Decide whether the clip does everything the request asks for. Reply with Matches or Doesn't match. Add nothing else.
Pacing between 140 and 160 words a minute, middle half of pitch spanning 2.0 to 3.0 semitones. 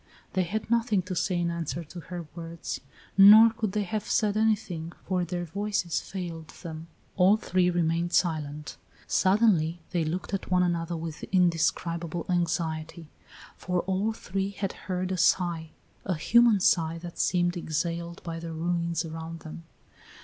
Matches